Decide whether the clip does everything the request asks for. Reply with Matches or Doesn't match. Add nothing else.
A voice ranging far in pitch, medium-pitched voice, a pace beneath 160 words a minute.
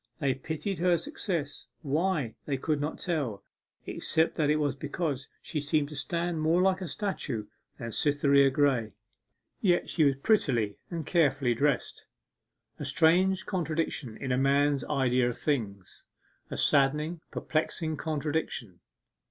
Doesn't match